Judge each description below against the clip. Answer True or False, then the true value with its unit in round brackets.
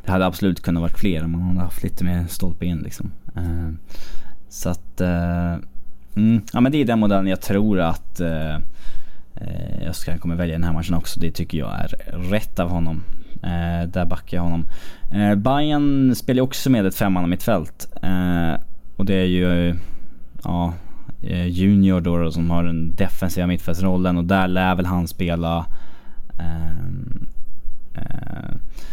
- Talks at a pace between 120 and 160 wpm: False (170 wpm)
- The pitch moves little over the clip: True (2.1 semitones)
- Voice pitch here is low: True (85 Hz)